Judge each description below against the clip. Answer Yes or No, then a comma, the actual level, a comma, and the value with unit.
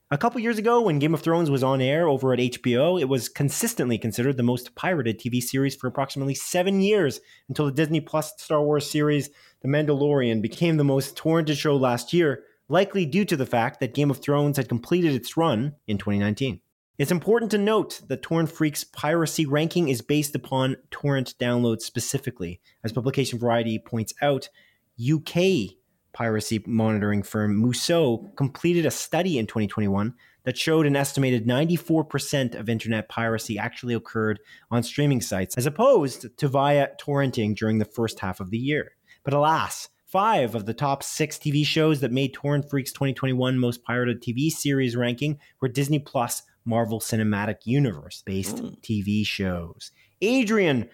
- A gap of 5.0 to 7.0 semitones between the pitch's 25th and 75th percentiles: No, average, 4.5 semitones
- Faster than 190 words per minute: No, average, 165 wpm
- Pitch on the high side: No, low, 135 Hz